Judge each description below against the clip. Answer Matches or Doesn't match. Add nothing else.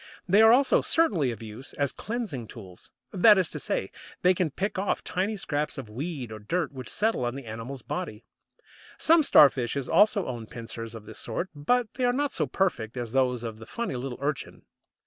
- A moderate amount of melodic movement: Doesn't match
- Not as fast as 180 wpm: Doesn't match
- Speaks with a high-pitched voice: Doesn't match